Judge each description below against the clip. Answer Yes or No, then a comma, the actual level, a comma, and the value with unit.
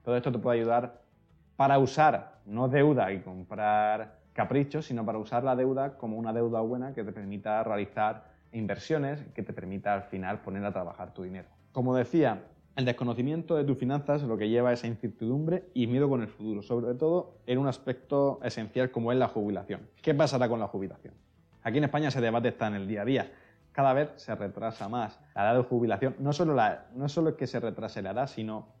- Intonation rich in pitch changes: No, average, 4.1 semitones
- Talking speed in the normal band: No, fast, 215 wpm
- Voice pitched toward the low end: Yes, low, 120 Hz